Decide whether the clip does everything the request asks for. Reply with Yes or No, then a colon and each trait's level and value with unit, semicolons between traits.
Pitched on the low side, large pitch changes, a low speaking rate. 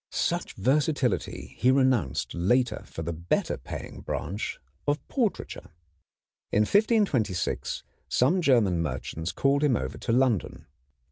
Yes: low, 120 Hz; wide, 7.9 semitones; slow, 120 wpm